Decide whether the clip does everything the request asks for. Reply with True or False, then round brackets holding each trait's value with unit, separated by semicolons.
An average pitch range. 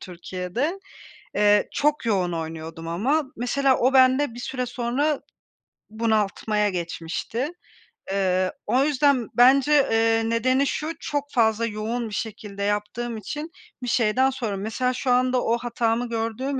True (3.9 semitones)